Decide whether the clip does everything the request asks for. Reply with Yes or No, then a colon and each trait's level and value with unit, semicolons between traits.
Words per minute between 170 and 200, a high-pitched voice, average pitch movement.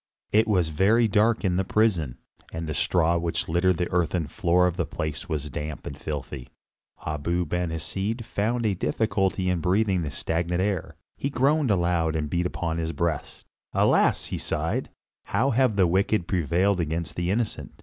No: average, 175 wpm; very low, 90 Hz; average, 3.9 semitones